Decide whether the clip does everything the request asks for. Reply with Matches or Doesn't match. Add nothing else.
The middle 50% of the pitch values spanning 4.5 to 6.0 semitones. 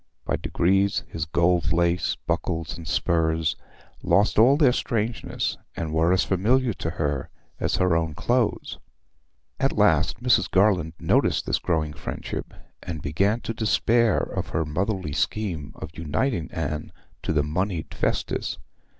Matches